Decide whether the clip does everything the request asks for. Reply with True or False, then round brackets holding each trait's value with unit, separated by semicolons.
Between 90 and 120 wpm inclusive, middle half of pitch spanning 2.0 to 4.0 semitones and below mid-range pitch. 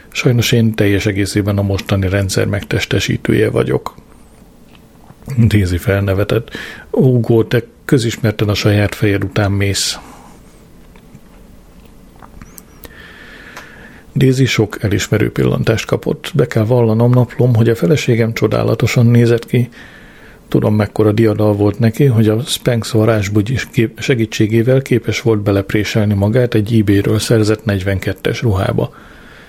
True (110 wpm; 2.5 semitones; 110 Hz)